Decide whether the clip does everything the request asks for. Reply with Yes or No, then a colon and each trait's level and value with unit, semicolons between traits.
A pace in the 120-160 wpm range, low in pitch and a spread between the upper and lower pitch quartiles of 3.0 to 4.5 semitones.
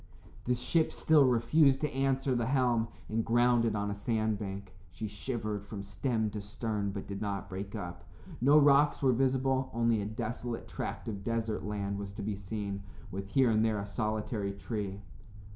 No: average, 175 wpm; low, 110 Hz; average, 3.5 semitones